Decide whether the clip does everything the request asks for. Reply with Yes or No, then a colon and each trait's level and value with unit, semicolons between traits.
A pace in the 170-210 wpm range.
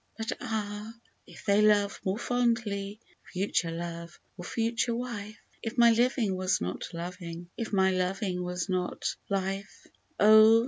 No: average, 145 wpm